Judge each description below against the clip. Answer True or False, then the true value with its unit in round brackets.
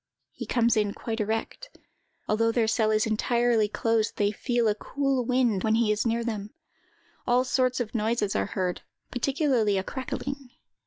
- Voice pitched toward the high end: True (230 Hz)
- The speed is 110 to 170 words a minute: True (165 wpm)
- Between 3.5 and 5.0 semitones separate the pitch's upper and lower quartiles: False (2.6 semitones)